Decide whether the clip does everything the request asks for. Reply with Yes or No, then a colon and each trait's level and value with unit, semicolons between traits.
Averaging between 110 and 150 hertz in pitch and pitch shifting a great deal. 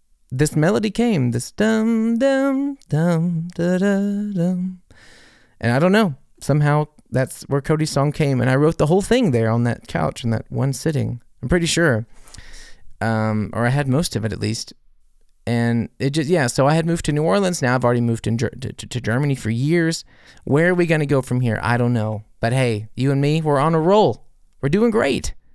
Yes: medium, 140 Hz; wide, 6.4 semitones